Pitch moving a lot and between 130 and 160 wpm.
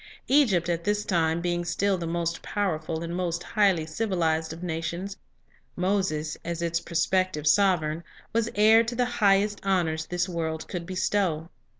No: average, 3.3 semitones; average, 155 wpm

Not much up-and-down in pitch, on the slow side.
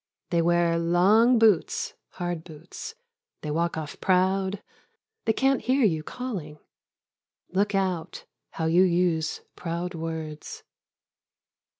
No: average, 3.7 semitones; slow, 120 wpm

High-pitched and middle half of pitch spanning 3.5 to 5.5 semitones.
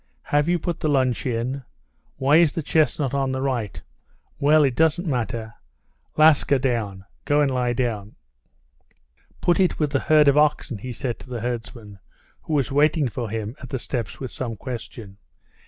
No: low, 130 Hz; average, 4.0 semitones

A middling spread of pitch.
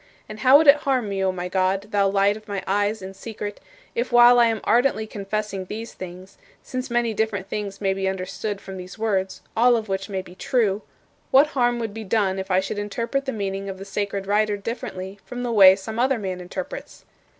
Yes: average, 3.0 semitones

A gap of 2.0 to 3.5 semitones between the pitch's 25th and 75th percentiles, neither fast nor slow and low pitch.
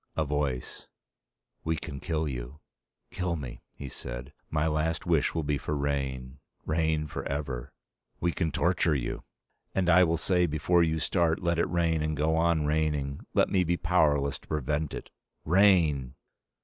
Yes: average, 2.8 semitones; average, 160 wpm; very low, 75 Hz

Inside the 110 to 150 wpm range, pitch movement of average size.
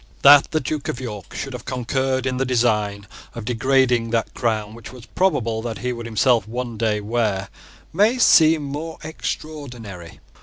No: average, 175 wpm; average, 3.5 semitones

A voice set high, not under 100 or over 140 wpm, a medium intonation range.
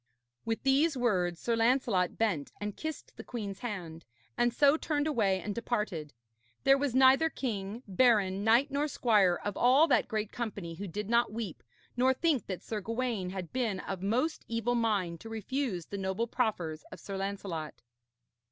No: high, 220 Hz; average, 170 wpm; average, 4.6 semitones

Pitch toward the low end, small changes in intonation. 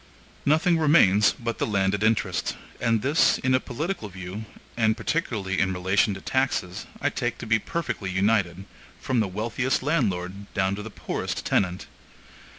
No: low, 110 Hz; average, 5.1 semitones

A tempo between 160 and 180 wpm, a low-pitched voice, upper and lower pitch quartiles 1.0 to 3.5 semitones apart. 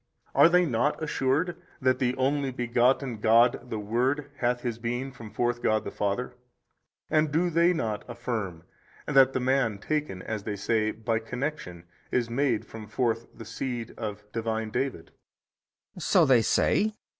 Yes: average, 165 wpm; low, 120 Hz; average, 3.2 semitones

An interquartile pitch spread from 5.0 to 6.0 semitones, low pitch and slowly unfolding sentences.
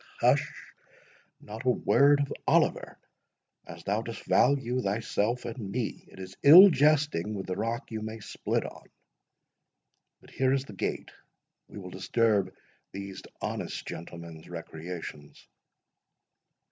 Yes: wide, 5.5 semitones; low, 110 Hz; slow, 120 wpm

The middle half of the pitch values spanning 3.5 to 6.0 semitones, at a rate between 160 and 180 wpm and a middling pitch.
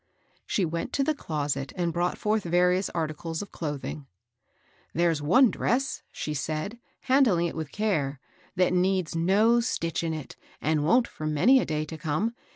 Yes: average, 5.0 semitones; average, 170 wpm; medium, 170 Hz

